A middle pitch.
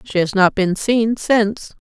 No: high, 205 Hz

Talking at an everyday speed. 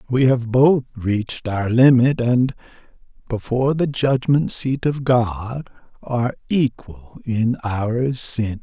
No: slow, 125 wpm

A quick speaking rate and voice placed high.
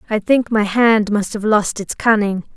Yes: fast, 210 wpm; high, 210 Hz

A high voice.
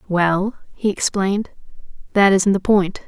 Yes: high, 195 Hz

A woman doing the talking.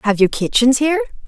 Yes: female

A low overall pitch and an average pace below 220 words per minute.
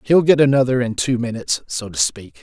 Yes: low, 125 Hz; average, 200 wpm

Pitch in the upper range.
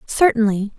Yes: high, 225 Hz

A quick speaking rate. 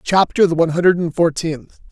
No: average, 190 wpm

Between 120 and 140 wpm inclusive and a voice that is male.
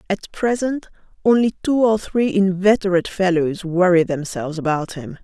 No: slow, 135 wpm; female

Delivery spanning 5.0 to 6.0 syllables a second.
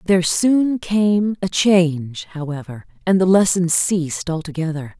No: 4.4 syllables/s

